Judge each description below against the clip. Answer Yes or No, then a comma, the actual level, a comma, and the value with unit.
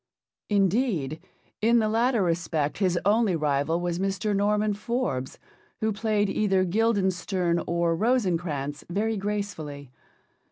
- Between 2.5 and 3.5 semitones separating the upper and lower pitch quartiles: No, average, 4.2 semitones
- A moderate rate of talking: No, slow, 115 wpm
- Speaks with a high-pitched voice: Yes, high, 195 Hz